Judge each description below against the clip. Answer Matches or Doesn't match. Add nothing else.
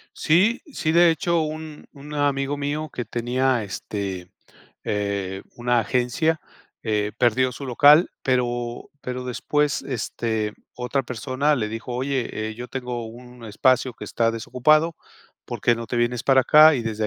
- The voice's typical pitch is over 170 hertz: Doesn't match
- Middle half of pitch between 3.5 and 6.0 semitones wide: Matches